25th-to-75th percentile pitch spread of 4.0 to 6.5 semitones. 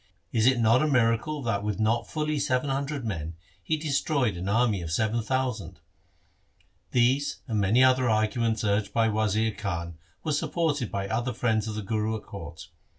No: average, 3.6 semitones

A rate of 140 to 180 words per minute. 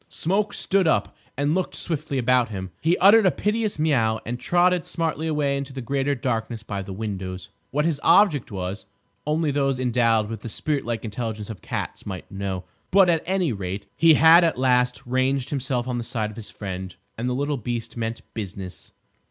No: average, 195 wpm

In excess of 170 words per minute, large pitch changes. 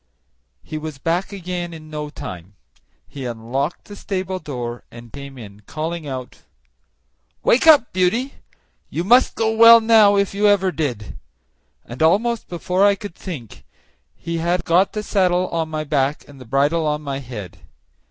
No: average, 160 wpm; wide, 6.0 semitones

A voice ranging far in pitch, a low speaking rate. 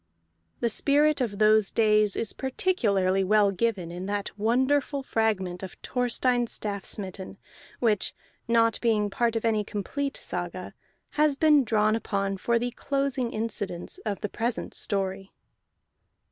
No: average, 3.6 semitones; slow, 130 wpm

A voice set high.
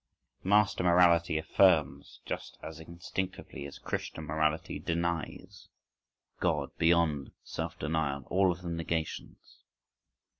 No: very low, 85 Hz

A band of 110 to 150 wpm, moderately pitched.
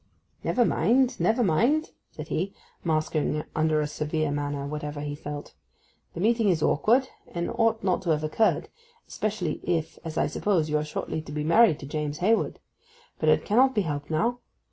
No: average, 180 wpm; medium, 160 Hz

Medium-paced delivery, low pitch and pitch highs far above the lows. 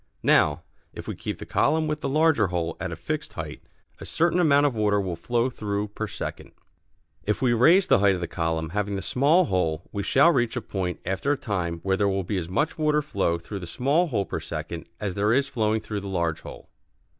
No: fast, 230 wpm; low, 105 Hz; wide, 6.9 semitones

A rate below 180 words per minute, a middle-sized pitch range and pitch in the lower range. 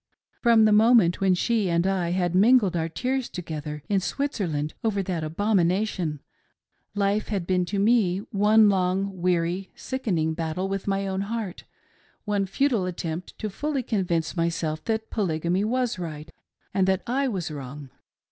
No: average, 160 wpm; average, 4.1 semitones; high, 190 Hz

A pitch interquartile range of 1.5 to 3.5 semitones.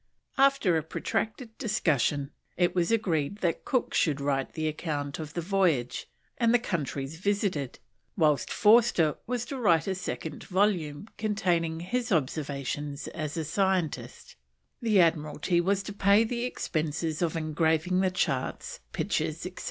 No: average, 5.1 semitones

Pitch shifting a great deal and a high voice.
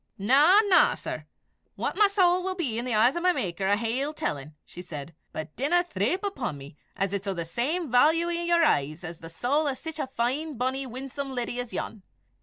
Yes: wide, 8.9 semitones; very high, 255 Hz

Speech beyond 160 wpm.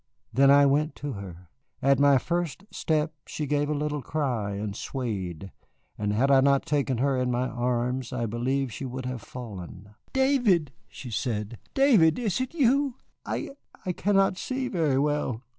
Yes: average, 170 wpm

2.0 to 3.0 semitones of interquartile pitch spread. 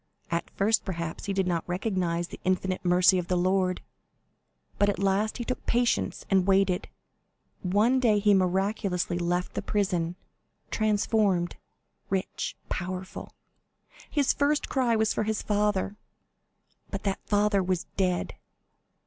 Yes: narrow, 2.6 semitones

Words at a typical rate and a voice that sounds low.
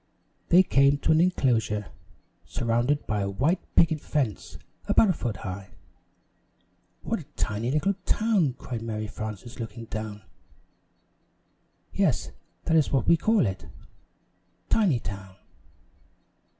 No: slow, 120 wpm; low, 120 Hz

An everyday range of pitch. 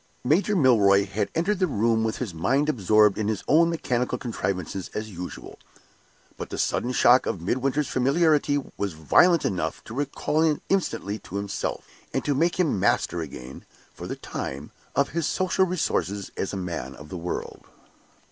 No: wide, 7.5 semitones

